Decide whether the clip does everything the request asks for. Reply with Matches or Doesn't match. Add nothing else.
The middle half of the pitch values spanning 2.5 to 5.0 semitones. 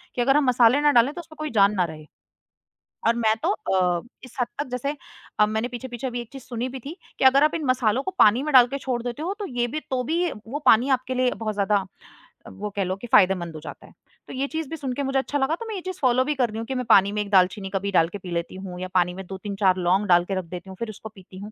Doesn't match